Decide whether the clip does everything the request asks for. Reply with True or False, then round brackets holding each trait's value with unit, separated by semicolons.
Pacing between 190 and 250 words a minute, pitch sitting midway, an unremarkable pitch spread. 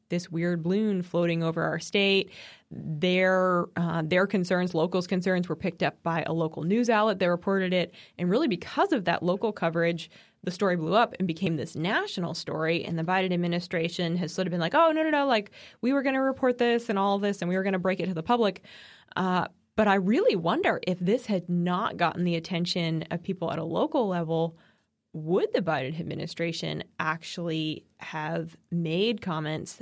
True (200 wpm; 180 Hz; 3.0 semitones)